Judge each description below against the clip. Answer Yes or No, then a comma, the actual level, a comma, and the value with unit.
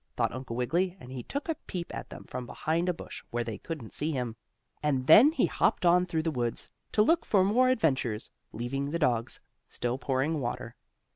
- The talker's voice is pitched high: No, medium, 145 Hz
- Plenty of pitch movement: Yes, wide, 6.5 semitones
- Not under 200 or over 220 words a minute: Yes, fast, 205 wpm